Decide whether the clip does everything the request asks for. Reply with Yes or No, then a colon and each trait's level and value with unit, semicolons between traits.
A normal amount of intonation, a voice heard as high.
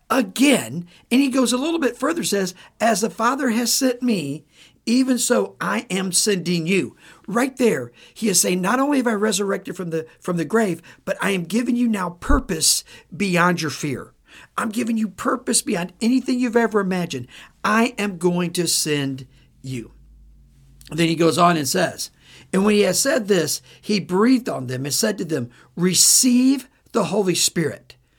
No: wide, 6.3 semitones; high, 195 Hz